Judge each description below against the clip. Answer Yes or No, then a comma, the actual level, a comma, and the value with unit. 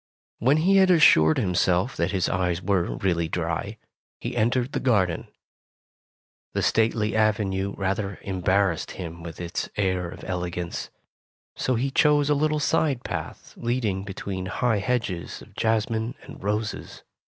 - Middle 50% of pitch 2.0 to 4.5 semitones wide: No, average, 5.0 semitones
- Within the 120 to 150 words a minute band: Yes, average, 140 wpm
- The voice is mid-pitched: No, low, 100 Hz